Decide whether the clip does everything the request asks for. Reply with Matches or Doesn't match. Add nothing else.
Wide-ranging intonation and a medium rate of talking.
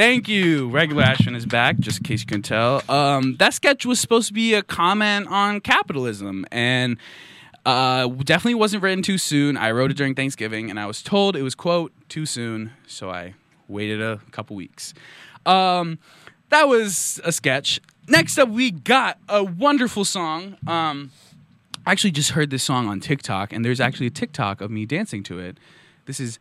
Matches